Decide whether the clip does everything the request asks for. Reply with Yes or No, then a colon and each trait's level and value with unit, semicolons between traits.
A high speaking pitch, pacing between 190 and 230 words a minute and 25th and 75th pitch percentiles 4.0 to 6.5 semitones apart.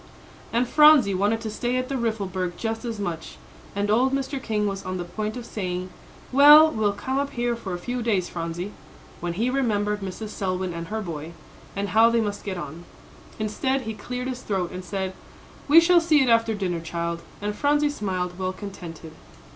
Yes: high, 210 Hz; average, 195 wpm; average, 4.9 semitones